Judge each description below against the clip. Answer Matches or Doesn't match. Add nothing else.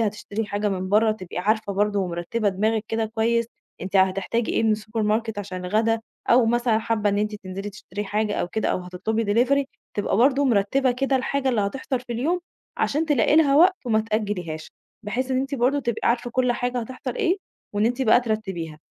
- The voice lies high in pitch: Matches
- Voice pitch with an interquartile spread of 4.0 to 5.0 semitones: Doesn't match